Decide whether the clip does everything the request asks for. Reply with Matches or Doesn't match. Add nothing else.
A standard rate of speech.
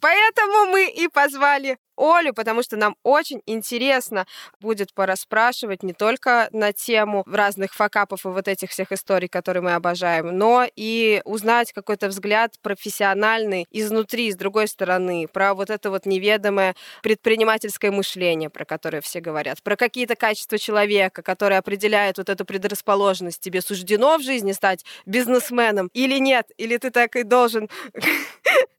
Matches